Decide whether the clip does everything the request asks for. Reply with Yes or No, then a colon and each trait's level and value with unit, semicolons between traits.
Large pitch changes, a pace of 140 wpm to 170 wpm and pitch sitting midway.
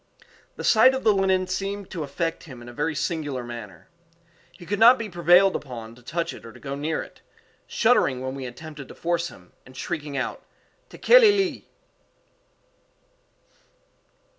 Yes: wide, 6.7 semitones; average, 165 wpm; medium, 160 Hz